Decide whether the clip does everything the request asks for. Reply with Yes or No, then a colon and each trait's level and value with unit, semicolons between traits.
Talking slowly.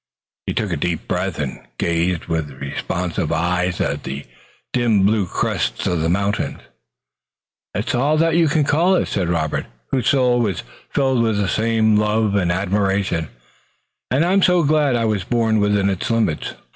No: average, 160 wpm